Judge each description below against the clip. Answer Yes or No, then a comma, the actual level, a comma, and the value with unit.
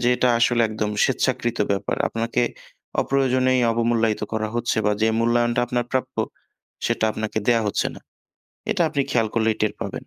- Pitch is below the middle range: Yes, low, 120 Hz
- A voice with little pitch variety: Yes, narrow, 2.1 semitones